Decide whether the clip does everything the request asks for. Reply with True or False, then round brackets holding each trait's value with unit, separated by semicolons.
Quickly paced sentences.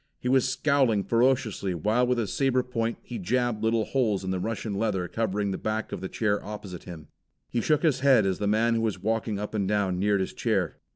True (225 wpm)